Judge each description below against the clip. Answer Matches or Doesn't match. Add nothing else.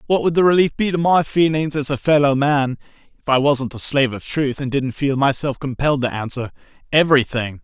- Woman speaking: Doesn't match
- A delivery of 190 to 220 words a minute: Matches